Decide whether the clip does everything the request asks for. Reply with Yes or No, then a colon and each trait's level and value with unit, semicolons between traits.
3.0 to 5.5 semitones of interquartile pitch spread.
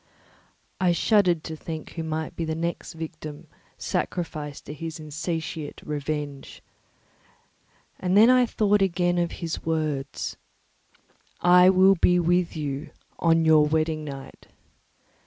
No: narrow, 2.4 semitones